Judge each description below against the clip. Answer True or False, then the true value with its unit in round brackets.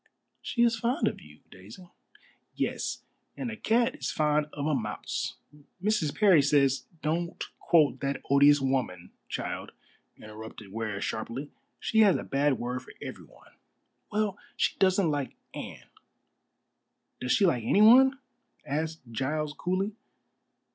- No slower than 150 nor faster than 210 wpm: False (135 wpm)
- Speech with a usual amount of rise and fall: False (6.9 semitones)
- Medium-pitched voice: True (150 Hz)